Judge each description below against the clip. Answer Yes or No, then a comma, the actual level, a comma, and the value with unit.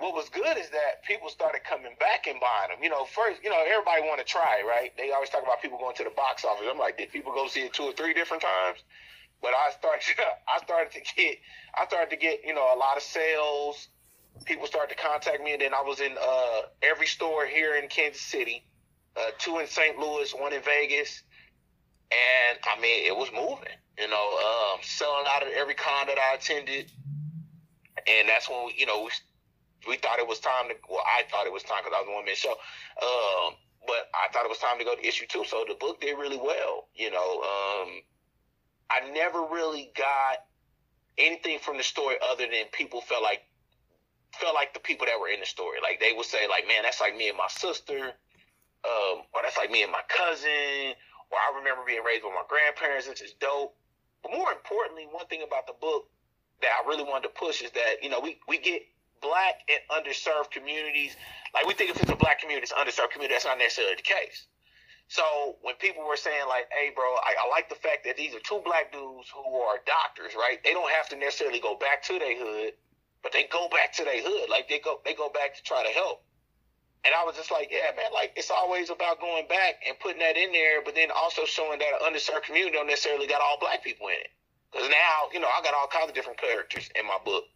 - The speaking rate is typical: No, fast, 235 wpm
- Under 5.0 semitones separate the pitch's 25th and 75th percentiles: No, average, 5.3 semitones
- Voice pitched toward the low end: No, medium, 150 Hz